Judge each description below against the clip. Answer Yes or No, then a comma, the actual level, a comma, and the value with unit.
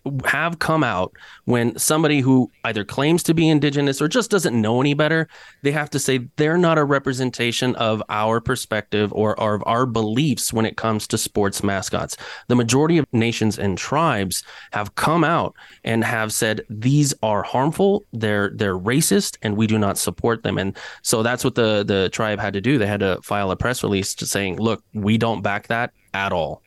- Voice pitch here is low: Yes, low, 115 Hz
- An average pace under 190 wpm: No, average, 200 wpm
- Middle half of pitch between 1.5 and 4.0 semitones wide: No, average, 5.2 semitones